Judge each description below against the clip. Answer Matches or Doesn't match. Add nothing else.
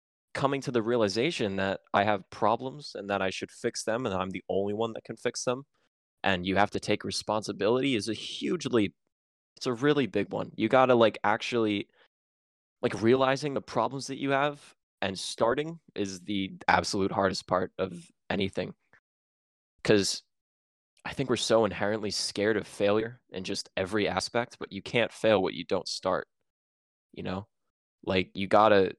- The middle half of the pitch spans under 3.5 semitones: Doesn't match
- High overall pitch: Doesn't match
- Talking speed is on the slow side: Doesn't match